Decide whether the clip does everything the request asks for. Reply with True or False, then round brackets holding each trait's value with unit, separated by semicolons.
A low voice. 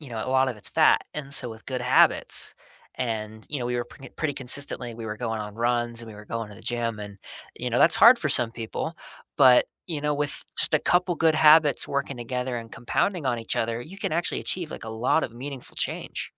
True (125 Hz)